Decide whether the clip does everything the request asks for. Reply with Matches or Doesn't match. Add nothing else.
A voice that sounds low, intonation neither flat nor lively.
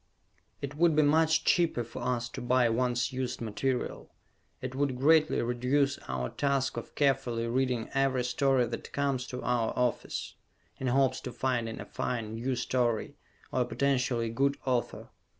Doesn't match